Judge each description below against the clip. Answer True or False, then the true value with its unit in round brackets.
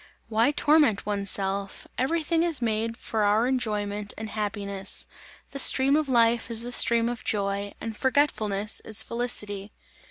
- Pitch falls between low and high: False (225 Hz)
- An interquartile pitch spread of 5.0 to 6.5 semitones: False (3.4 semitones)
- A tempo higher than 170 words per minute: False (155 wpm)